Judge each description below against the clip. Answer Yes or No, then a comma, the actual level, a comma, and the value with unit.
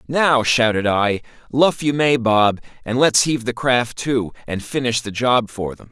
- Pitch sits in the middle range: No, low, 120 Hz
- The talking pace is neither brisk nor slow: Yes, average, 195 wpm